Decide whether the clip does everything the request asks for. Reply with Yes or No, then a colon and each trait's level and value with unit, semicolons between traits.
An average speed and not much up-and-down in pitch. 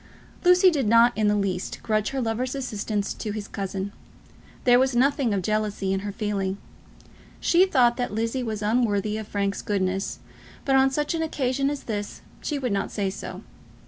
No: average, 180 wpm; average, 4.5 semitones